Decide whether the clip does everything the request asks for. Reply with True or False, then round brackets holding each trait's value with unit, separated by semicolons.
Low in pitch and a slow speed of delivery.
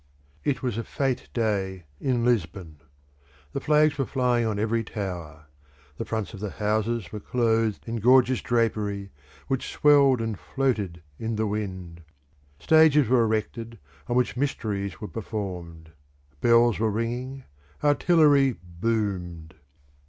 True (115 Hz; 130 wpm)